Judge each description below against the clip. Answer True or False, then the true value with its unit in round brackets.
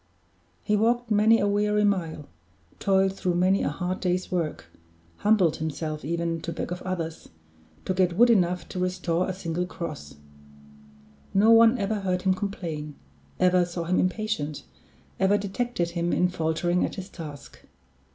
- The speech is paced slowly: False (155 wpm)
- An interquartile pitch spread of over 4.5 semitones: False (3.2 semitones)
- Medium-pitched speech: True (180 Hz)